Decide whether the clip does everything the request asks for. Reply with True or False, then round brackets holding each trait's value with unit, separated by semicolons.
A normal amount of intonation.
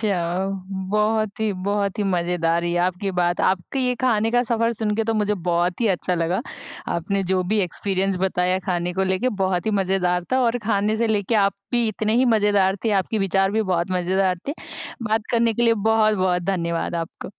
True (3.3 semitones)